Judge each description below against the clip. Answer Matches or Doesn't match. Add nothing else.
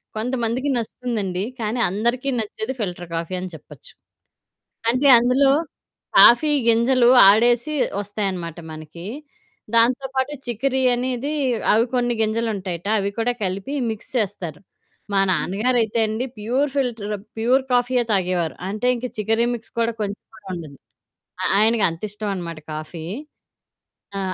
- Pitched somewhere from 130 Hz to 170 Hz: Doesn't match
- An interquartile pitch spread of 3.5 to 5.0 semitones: Matches